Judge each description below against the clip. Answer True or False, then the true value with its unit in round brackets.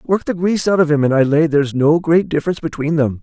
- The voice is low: False (155 Hz)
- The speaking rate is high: True (280 wpm)